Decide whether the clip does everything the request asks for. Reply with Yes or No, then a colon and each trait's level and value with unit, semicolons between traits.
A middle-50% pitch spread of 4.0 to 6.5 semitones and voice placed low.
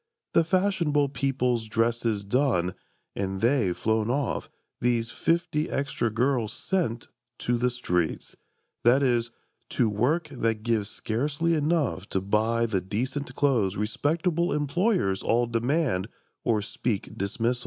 Yes: average, 4.9 semitones; low, 120 Hz